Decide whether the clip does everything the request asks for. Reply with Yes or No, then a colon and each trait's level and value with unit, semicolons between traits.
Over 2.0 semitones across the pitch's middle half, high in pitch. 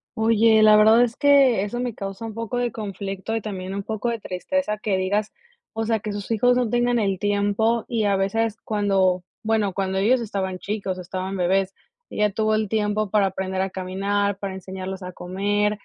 Yes: narrow, 2.5 semitones; high, 205 Hz